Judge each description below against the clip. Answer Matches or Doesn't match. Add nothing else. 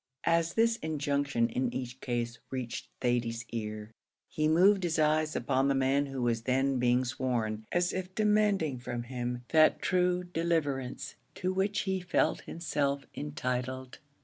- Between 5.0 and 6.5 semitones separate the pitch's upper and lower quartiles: Matches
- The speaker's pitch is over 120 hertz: Matches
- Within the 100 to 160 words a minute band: Matches